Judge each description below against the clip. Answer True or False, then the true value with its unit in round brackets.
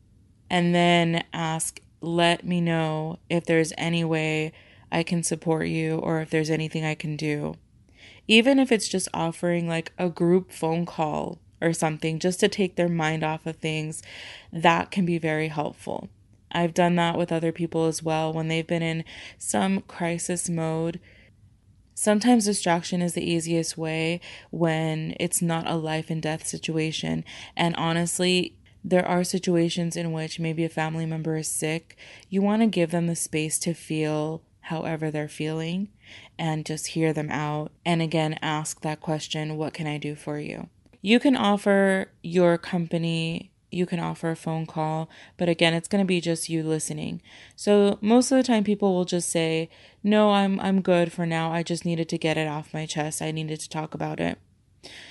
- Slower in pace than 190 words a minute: True (180 wpm)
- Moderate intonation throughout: False (1.8 semitones)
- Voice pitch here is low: False (165 Hz)